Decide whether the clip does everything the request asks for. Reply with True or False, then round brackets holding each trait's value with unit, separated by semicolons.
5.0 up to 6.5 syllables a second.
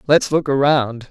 False (4.1 syllables/s)